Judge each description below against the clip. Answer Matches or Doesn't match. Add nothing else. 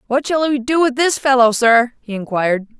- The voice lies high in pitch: Matches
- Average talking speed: Doesn't match